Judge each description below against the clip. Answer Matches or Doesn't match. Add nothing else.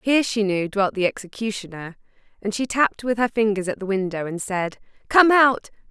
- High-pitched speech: Matches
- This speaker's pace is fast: Doesn't match